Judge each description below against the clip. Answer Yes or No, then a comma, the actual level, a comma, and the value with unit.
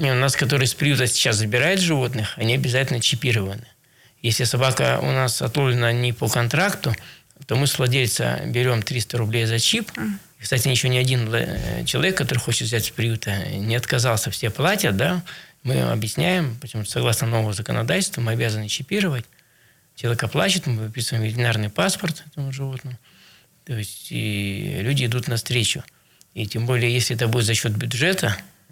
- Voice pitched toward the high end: No, low, 125 Hz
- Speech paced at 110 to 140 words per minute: No, fast, 160 wpm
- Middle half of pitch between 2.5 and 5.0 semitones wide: Yes, average, 3.1 semitones